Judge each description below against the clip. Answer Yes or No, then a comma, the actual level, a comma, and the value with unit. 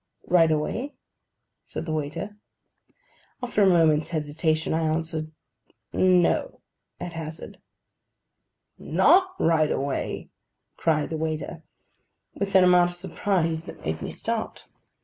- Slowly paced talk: Yes, slow, 115 wpm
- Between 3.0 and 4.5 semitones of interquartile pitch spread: No, narrow, 2.5 semitones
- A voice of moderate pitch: Yes, medium, 165 Hz